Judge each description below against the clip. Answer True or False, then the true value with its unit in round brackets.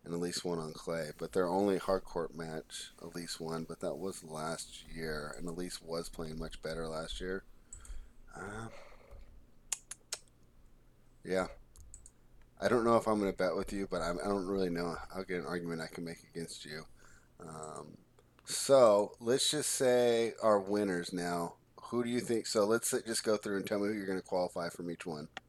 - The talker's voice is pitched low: True (85 Hz)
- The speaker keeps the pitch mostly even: False (3.6 semitones)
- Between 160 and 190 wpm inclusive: True (185 wpm)